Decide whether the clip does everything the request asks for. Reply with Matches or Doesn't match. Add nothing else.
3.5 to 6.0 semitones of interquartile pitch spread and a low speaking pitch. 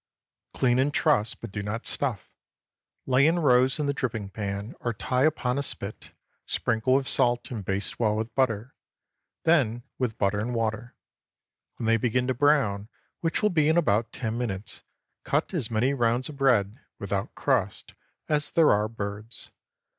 Matches